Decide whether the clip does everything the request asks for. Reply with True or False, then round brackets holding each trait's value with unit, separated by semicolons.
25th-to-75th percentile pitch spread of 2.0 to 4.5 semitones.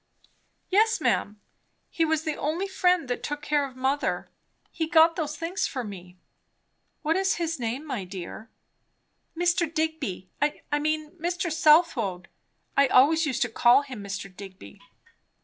False (5.5 semitones)